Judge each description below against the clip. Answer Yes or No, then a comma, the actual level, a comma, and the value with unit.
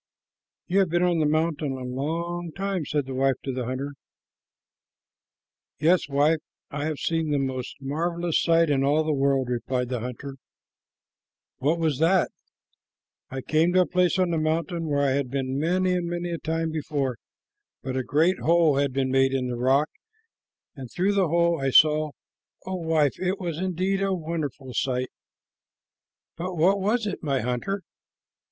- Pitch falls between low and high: Yes, medium, 155 Hz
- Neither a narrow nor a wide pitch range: Yes, average, 4.2 semitones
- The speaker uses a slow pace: No, average, 175 wpm